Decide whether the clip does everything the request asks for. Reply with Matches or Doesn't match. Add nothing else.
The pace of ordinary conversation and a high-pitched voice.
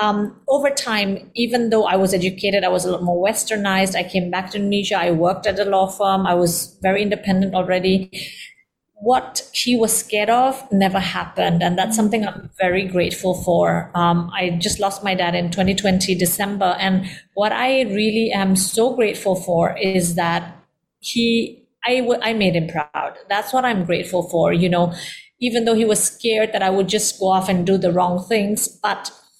Matches